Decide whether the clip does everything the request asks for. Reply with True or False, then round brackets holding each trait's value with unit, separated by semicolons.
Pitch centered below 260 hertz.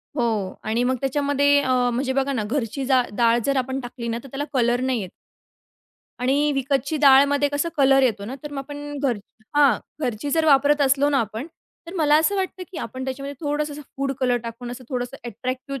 False (270 Hz)